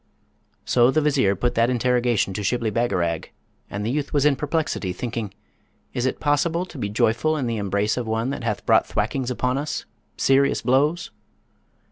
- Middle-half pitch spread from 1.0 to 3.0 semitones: No, average, 4.3 semitones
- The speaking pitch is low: Yes, low, 125 Hz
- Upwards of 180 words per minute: No, average, 175 wpm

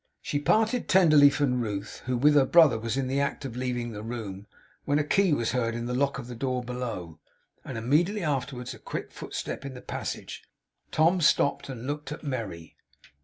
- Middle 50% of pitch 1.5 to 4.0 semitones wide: Yes, average, 3.7 semitones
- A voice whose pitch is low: Yes, low, 130 Hz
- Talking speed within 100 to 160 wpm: No, average, 200 wpm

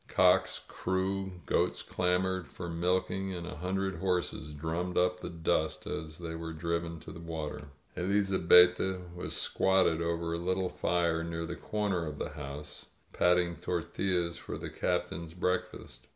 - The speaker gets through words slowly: No, average, 145 wpm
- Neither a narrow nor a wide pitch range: No, narrow, 1.9 semitones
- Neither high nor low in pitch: No, very low, 90 Hz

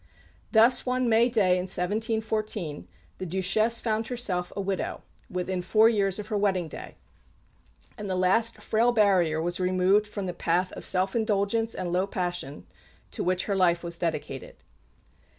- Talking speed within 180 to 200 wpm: No, average, 160 wpm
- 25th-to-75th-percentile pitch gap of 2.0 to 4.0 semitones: Yes, average, 3.4 semitones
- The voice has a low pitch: No, high, 195 Hz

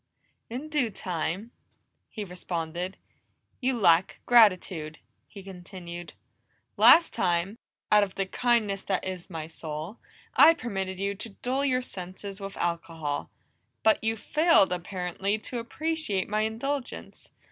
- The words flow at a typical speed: No, slow, 125 wpm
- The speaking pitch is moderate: No, high, 195 Hz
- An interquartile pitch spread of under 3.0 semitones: No, average, 4.6 semitones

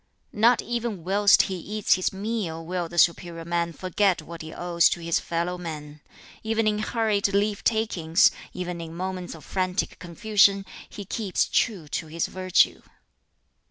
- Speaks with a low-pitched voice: No, medium, 185 Hz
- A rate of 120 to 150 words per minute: No, average, 160 wpm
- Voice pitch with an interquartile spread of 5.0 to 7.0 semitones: No, average, 3.5 semitones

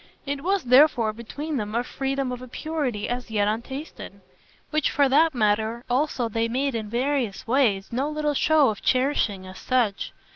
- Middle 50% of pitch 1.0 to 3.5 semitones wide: No, average, 4.2 semitones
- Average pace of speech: Yes, average, 175 wpm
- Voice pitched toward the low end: No, very high, 255 Hz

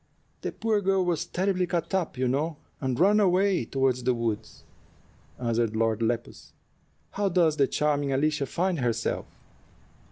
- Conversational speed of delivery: Yes, average, 150 wpm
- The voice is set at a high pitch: No, medium, 150 Hz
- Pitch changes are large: Yes, wide, 6.9 semitones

